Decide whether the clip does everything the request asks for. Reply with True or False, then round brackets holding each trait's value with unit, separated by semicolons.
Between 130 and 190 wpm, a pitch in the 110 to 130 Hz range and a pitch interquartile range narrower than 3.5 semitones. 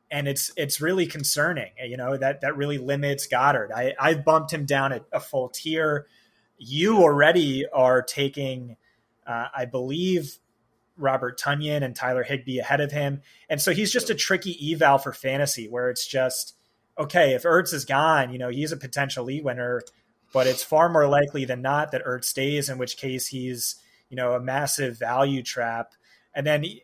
False (185 wpm; 140 Hz; 2.8 semitones)